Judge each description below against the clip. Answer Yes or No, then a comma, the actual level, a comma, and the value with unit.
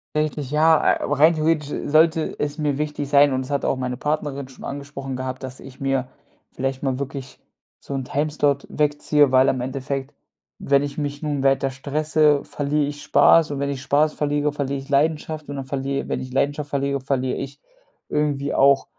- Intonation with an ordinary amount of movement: No, narrow, 1.6 semitones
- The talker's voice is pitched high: No, medium, 140 Hz